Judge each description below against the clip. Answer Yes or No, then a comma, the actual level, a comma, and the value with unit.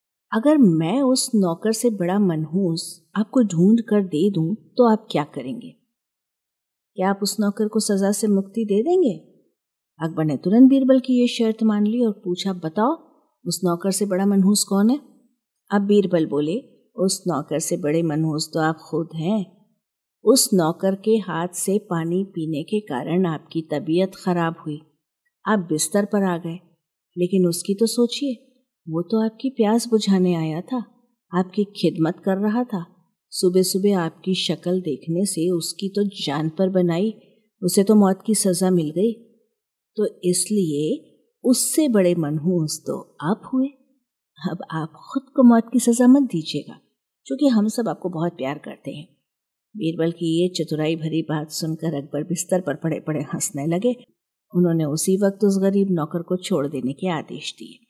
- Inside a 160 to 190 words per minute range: Yes, average, 165 wpm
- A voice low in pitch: No, high, 190 Hz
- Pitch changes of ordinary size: Yes, average, 5.0 semitones